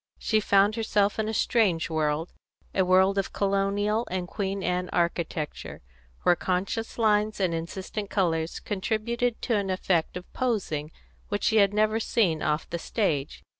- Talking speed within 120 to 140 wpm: No, average, 155 wpm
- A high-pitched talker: Yes, high, 195 Hz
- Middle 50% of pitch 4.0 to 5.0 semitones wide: No, average, 3.6 semitones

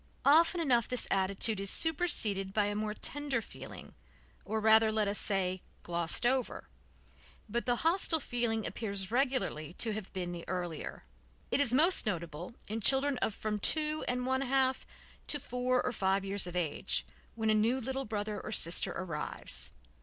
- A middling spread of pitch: Yes, average, 5.0 semitones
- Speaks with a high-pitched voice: Yes, high, 220 Hz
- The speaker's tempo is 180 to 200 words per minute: No, average, 170 wpm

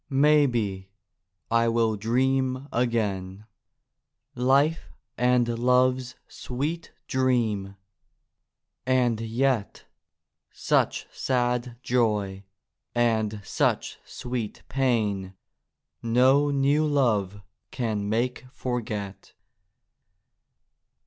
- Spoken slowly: Yes, slow, 70 wpm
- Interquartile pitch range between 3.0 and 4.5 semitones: Yes, average, 3.3 semitones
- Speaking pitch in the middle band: No, low, 120 Hz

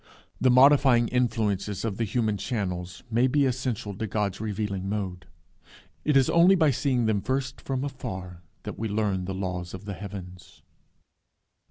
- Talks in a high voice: No, low, 110 Hz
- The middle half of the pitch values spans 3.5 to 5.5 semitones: Yes, average, 5.0 semitones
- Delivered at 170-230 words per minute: No, average, 160 wpm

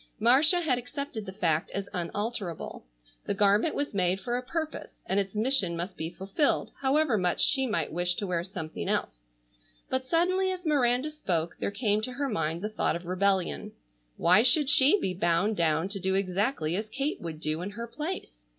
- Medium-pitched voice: No, high, 205 Hz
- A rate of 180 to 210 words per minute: Yes, average, 190 wpm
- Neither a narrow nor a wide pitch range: No, wide, 7.0 semitones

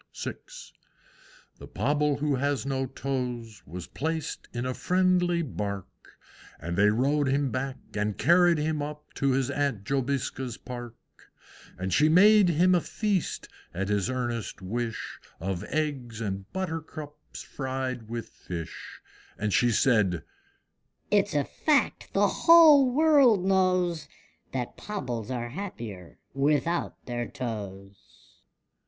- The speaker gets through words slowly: Yes, slow, 125 wpm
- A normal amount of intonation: No, wide, 6.3 semitones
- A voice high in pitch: No, low, 135 Hz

